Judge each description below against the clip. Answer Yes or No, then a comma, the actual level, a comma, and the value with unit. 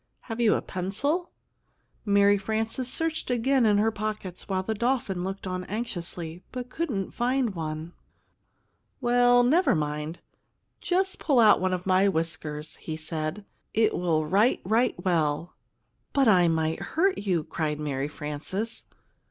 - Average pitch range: No, wide, 6.5 semitones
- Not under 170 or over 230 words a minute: No, average, 145 wpm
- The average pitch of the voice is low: No, high, 195 Hz